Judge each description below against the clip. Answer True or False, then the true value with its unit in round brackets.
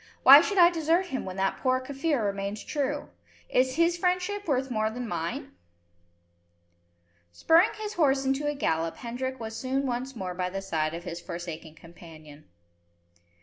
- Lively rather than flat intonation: True (8.2 semitones)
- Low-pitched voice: False (255 Hz)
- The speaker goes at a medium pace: True (160 wpm)